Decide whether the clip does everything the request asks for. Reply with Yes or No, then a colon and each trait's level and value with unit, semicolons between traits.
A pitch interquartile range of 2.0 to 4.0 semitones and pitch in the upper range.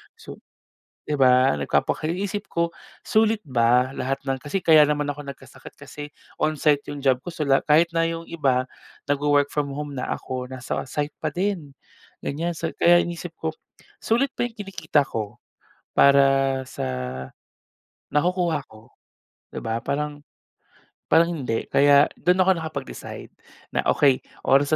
No: average, 3.7 semitones; medium, 145 Hz